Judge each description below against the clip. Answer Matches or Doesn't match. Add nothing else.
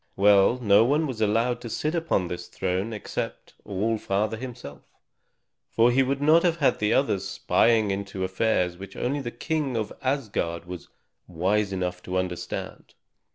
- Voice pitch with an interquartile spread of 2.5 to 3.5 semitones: Doesn't match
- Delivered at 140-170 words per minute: Matches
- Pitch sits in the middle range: Doesn't match